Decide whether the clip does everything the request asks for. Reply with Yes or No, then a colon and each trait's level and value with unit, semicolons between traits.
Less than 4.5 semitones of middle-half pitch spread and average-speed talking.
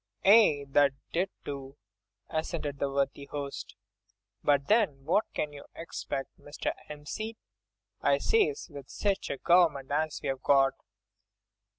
No: average, 4.0 semitones; slow, 125 wpm